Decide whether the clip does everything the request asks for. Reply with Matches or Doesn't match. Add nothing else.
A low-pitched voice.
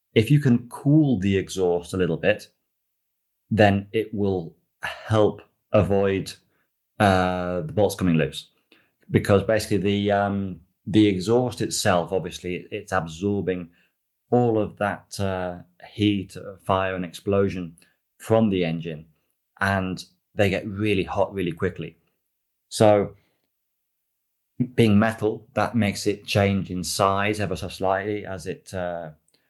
Matches